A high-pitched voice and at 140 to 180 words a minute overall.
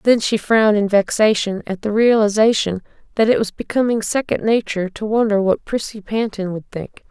Yes: high, 210 Hz; average, 175 wpm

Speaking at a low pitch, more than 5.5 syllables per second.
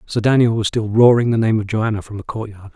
Yes: low, 110 Hz; 6.1 syllables/s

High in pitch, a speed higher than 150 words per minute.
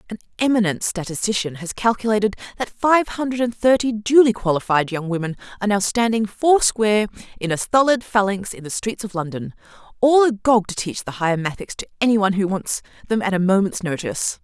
Yes: high, 205 Hz; average, 185 wpm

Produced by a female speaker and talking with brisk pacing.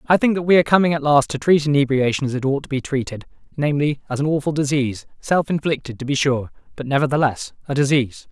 No: male; fast, 225 wpm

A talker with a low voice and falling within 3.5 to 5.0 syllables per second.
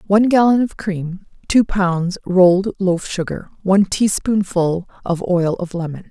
No: high, 190 Hz; 4.4 syllables/s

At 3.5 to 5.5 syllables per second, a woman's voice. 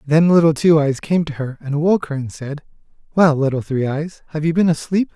No: 5.2 syllables/s; male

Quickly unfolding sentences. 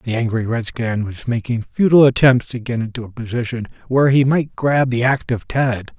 No: average, 190 wpm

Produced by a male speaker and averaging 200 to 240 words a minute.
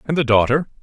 Yes: male; fast, 220 wpm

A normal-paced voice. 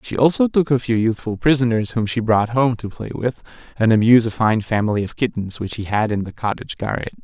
No: fast, 230 wpm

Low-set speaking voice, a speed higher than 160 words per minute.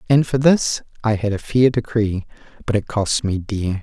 Yes: low, 110 Hz; fast, 205 wpm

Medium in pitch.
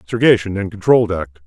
No: low, 100 Hz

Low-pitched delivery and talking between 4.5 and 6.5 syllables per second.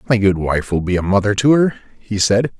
Yes: low, 105 Hz; 5.7 syllables/s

